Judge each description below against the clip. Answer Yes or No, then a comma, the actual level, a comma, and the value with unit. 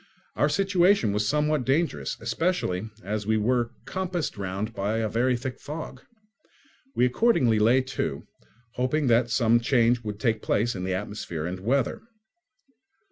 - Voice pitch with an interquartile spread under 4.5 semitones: No, average, 4.8 semitones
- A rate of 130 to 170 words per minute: Yes, average, 145 wpm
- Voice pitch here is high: No, low, 120 Hz